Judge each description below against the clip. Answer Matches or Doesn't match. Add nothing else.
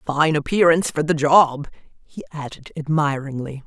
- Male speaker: Doesn't match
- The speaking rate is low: Matches